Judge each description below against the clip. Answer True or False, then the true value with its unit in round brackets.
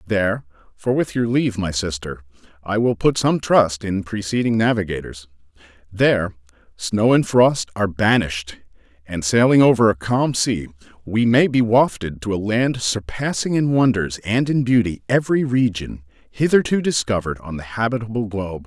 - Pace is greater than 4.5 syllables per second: True (5.1 syllables/s)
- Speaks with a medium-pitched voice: False (105 Hz)